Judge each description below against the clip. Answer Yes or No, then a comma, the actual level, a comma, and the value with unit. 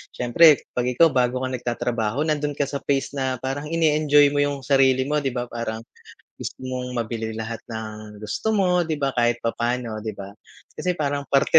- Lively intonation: No, average, 3.7 semitones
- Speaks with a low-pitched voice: Yes, low, 130 Hz